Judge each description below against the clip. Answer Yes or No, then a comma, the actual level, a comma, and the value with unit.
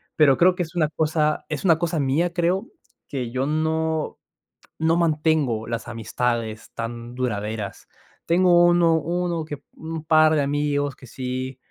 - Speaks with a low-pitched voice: No, medium, 155 Hz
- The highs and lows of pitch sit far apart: No, average, 4.3 semitones